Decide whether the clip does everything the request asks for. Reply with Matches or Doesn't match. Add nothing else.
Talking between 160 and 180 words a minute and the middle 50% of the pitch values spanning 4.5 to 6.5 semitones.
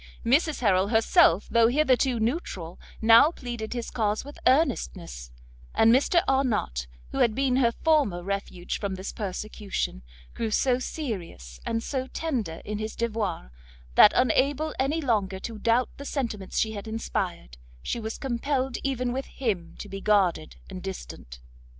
Doesn't match